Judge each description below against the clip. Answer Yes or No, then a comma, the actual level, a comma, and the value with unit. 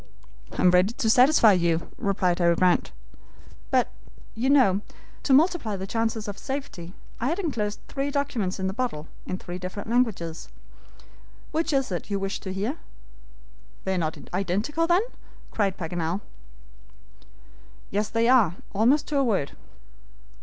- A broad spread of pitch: Yes, wide, 6.1 semitones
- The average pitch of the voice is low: No, high, 210 Hz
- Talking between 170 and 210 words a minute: No, average, 150 wpm